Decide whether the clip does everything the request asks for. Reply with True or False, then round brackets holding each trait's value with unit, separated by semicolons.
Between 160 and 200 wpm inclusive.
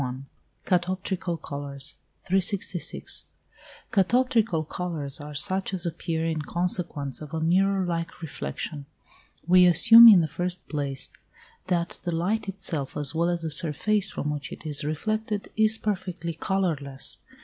False (140 wpm)